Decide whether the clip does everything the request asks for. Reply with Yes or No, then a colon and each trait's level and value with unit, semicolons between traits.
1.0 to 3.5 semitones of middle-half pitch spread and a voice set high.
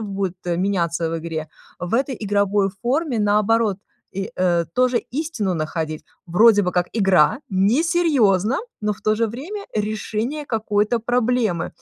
No: average, 4.5 semitones; high, 210 Hz